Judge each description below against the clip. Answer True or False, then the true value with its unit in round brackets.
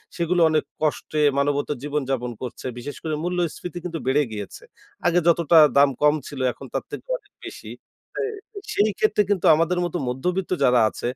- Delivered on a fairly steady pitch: False (4.0 semitones)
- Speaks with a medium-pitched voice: True (155 Hz)